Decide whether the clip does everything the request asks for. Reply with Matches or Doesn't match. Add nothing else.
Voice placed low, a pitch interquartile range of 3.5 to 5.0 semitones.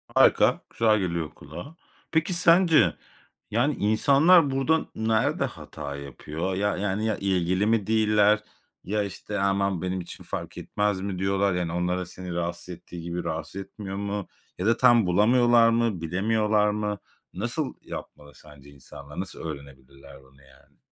Matches